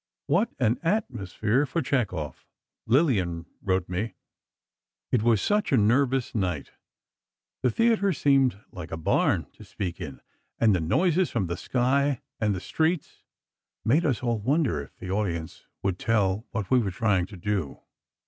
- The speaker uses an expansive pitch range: Yes, wide, 6.6 semitones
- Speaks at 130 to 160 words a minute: Yes, average, 155 wpm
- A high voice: No, low, 110 Hz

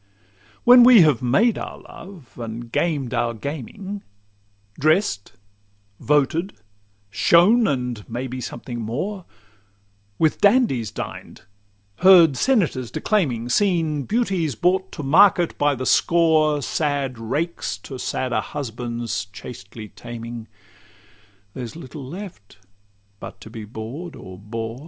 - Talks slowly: Yes, slow, 115 wpm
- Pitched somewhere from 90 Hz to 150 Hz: Yes, medium, 140 Hz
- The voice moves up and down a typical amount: No, wide, 6.7 semitones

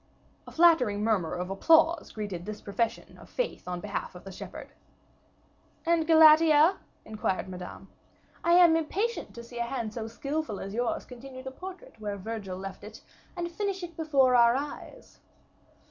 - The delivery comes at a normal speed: Yes, average, 160 wpm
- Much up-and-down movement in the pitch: Yes, wide, 7.8 semitones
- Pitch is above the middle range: Yes, high, 245 Hz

